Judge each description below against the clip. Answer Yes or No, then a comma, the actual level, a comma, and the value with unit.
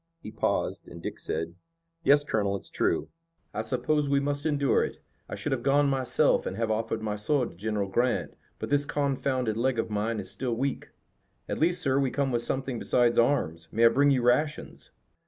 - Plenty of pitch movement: No, average, 4.1 semitones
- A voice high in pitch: No, low, 125 Hz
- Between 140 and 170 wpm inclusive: No, average, 200 wpm